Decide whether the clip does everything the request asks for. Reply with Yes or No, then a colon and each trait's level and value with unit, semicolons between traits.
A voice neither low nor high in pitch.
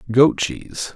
No: low, 130 Hz